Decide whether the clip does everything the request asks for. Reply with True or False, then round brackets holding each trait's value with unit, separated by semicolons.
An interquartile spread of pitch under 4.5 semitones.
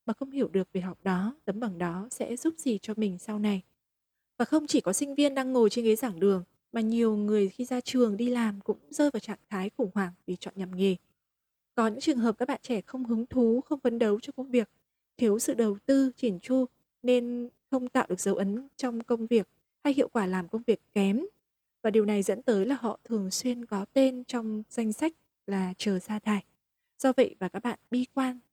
True (4.0 semitones)